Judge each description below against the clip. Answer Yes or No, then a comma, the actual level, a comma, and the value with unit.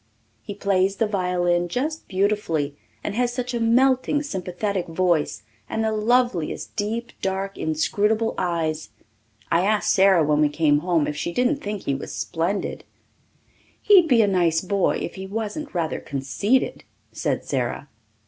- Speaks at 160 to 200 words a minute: No, average, 150 wpm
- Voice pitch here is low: No, high, 195 Hz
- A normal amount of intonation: Yes, average, 4.9 semitones